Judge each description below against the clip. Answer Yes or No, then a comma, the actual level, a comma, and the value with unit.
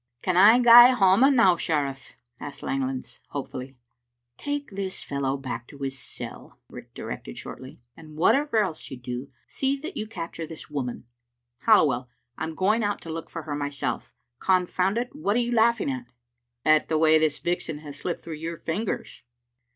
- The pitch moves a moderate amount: No, wide, 7.5 semitones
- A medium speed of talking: Yes, average, 180 wpm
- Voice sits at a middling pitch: Yes, medium, 165 Hz